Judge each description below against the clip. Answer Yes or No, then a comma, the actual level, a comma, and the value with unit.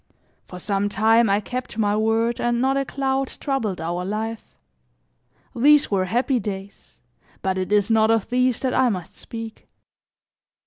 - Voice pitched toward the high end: Yes, high, 225 Hz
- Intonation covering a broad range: No, average, 3.8 semitones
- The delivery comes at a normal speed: Yes, average, 160 wpm